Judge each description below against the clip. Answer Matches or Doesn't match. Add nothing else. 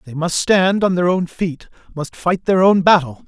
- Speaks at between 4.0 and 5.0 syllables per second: Matches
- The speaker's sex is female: Doesn't match